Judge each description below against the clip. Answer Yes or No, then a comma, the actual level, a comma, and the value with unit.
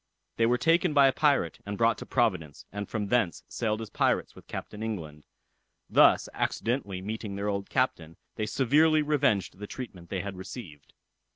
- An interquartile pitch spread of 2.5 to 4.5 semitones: No, average, 5.0 semitones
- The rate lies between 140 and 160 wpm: No, average, 175 wpm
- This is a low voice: Yes, low, 105 Hz